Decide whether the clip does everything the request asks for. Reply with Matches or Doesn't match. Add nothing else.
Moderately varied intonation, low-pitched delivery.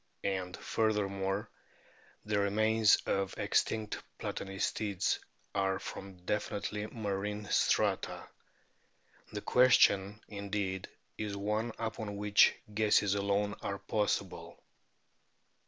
Doesn't match